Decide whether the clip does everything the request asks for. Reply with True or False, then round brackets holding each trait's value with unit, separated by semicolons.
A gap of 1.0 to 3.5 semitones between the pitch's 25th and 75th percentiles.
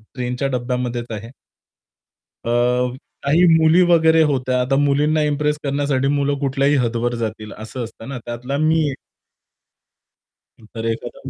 True (3.0 semitones)